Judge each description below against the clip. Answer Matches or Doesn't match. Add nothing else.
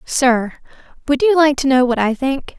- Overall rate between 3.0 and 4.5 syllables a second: Matches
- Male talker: Doesn't match